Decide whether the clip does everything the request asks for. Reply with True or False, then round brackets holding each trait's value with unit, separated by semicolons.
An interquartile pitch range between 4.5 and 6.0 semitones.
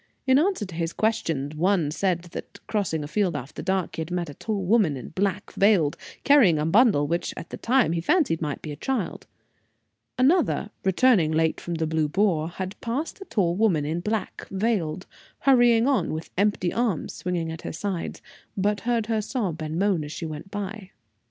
True (5.2 semitones)